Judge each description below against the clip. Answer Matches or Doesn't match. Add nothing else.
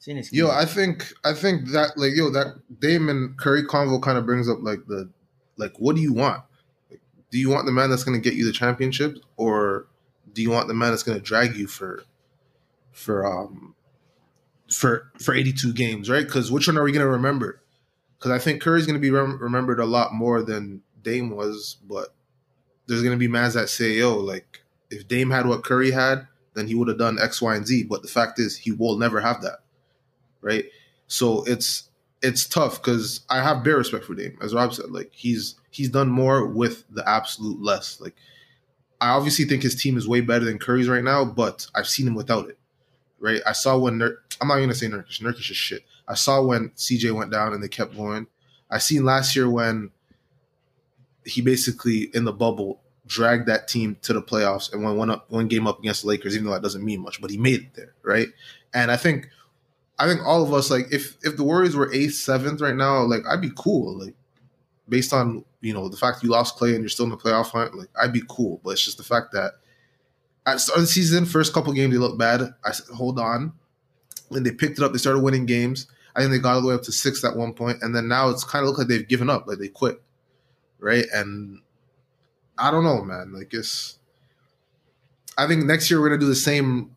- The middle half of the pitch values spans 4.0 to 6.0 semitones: Doesn't match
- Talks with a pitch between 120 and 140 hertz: Matches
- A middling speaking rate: Doesn't match